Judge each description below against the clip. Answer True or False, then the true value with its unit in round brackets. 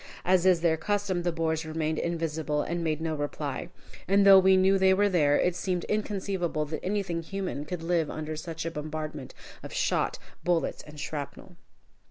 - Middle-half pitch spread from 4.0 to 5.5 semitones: False (3.2 semitones)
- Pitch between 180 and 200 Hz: False (165 Hz)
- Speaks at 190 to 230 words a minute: False (180 wpm)